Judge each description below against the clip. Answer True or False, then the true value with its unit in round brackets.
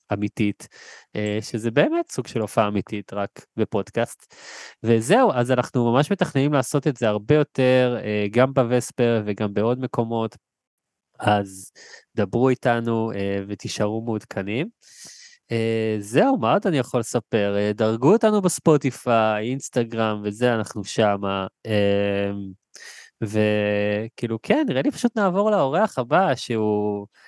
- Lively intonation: False (3.9 semitones)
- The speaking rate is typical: True (110 wpm)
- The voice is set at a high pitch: False (115 Hz)